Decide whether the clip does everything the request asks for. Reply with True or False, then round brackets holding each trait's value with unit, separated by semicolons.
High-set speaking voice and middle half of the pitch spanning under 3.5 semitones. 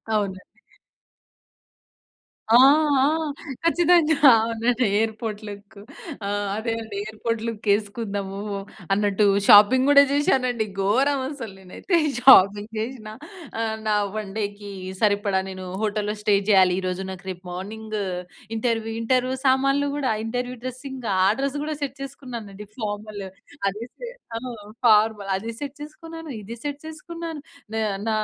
False (225 Hz; 4.3 semitones)